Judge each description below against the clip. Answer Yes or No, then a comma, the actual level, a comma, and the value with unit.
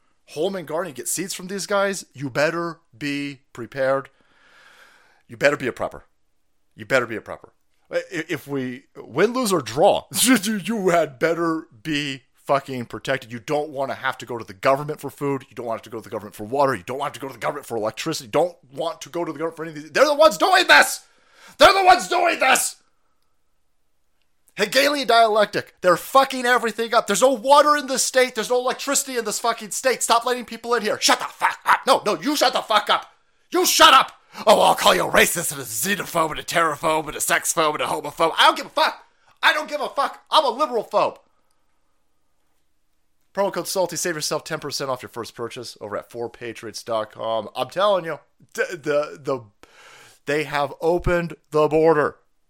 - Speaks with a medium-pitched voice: Yes, medium, 160 Hz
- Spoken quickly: Yes, fast, 210 wpm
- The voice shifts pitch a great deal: Yes, wide, 9.0 semitones